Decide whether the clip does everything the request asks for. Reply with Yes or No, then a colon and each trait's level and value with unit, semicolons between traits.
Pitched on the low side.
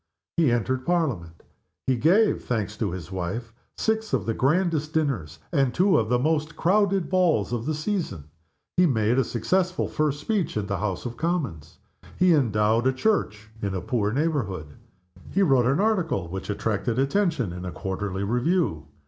Yes: low, 125 Hz